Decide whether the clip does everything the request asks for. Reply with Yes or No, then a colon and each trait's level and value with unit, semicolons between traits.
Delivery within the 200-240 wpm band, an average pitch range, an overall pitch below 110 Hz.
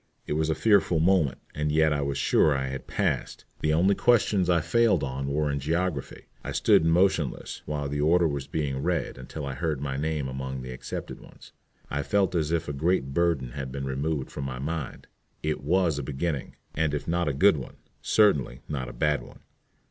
Yes: fast, 205 wpm; average, 3.6 semitones; very low, 75 Hz